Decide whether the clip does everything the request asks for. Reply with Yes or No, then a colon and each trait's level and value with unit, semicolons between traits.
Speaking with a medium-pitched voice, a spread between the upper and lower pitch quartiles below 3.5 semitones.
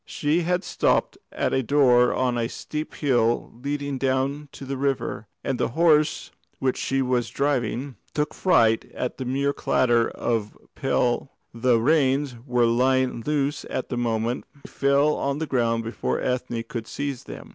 No: low, 130 Hz; average, 2.9 semitones